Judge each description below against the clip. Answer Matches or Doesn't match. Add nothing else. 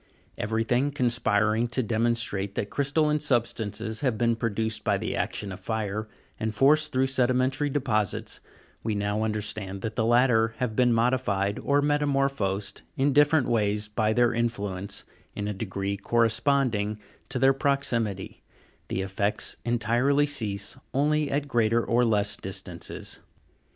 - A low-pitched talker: Matches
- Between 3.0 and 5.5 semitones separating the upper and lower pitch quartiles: Matches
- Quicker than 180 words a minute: Doesn't match